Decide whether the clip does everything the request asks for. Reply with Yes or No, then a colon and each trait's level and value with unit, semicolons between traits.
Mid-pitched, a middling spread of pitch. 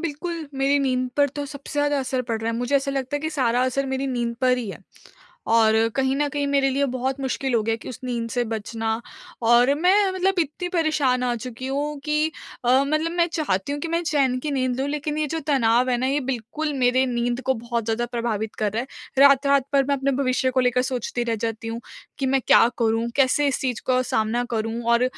No: very high, 260 Hz; average, 3.1 semitones